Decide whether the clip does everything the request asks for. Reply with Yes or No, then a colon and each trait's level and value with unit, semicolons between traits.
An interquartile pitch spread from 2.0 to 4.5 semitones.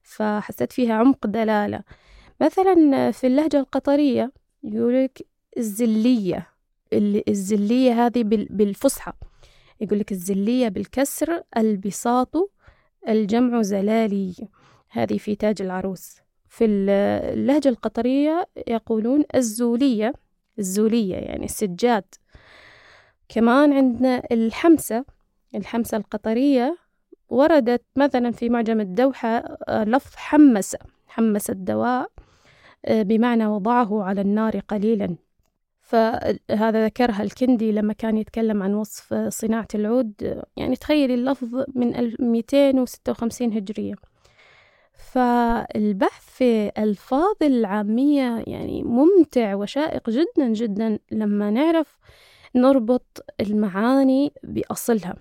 Yes: average, 3.7 semitones